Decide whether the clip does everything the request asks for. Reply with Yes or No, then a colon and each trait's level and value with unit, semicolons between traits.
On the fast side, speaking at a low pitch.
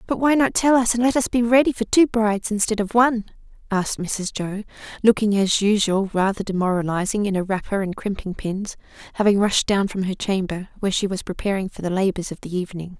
No: fast, 210 wpm; high, 205 Hz